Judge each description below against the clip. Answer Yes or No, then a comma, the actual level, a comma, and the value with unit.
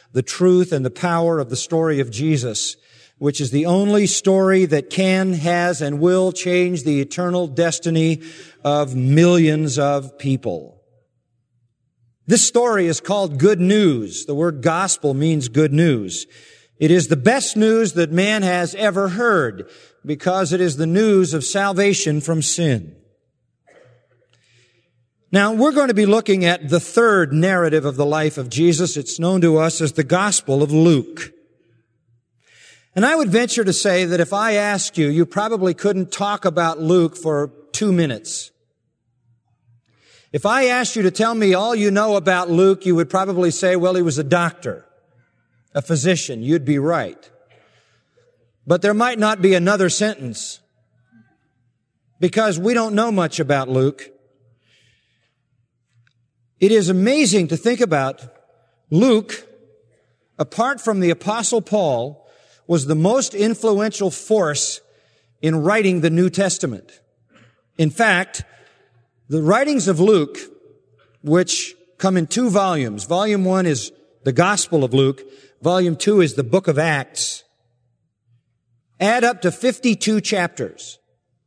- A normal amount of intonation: No, wide, 6.0 semitones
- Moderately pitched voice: Yes, medium, 170 Hz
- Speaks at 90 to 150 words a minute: Yes, average, 145 wpm